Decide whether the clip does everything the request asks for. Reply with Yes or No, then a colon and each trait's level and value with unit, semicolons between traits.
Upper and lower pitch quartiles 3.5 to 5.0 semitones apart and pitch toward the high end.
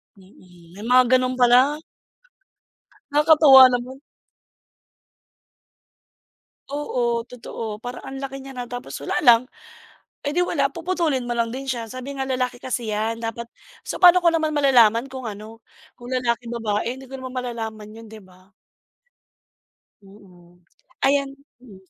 No: average, 3.0 semitones; high, 245 Hz